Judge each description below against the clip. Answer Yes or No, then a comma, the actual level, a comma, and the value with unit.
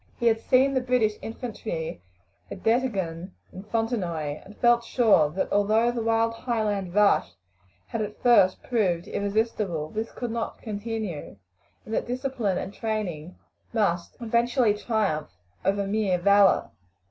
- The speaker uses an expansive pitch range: No, average, 3.7 semitones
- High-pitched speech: Yes, high, 215 Hz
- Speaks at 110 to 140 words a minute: Yes, slow, 135 wpm